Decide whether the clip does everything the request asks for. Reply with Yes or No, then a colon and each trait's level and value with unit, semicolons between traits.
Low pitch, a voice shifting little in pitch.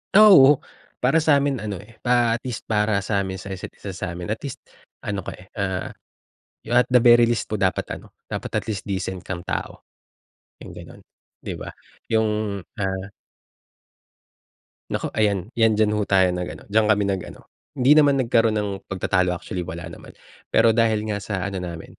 No: low, 105 Hz; average, 3.4 semitones